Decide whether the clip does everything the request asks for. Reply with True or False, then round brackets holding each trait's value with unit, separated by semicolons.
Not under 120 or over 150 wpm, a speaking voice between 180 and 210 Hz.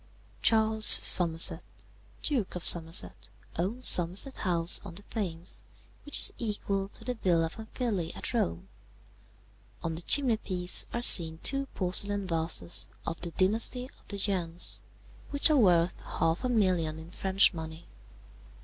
True (140 wpm; 185 Hz)